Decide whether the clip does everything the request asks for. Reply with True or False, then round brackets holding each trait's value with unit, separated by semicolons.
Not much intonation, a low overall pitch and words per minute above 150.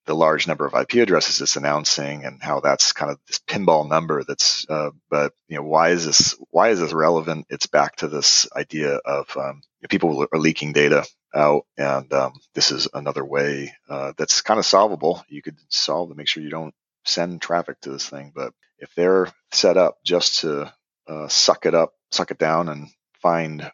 True (1.8 semitones; 75 Hz; 200 wpm)